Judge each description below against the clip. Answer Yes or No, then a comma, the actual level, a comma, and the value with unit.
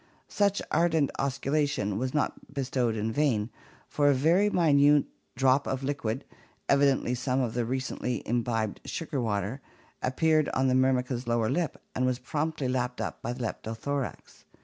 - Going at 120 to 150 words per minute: No, average, 160 wpm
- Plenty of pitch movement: No, average, 2.9 semitones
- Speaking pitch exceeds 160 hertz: No, low, 130 Hz